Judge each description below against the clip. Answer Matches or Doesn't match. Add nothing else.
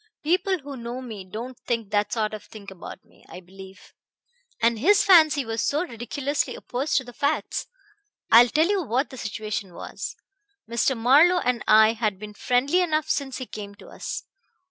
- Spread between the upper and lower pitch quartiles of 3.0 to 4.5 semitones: Doesn't match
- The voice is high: Matches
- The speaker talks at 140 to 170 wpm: Doesn't match